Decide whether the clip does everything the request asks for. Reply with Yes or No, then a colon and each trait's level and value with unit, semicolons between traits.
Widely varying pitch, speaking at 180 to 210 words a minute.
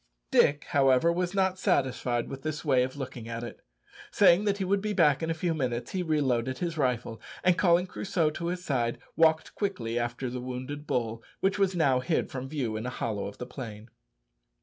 Yes: wide, 5.8 semitones; fast, 205 wpm